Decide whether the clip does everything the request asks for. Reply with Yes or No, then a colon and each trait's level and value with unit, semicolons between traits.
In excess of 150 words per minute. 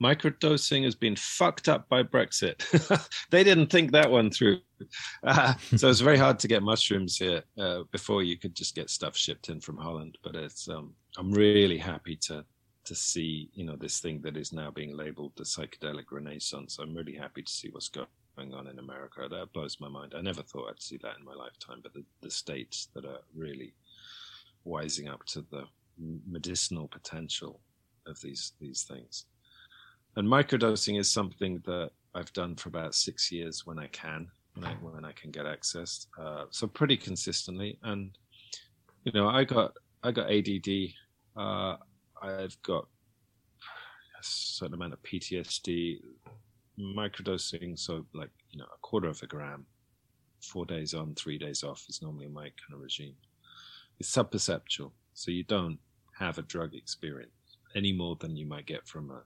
Yes: average, 175 wpm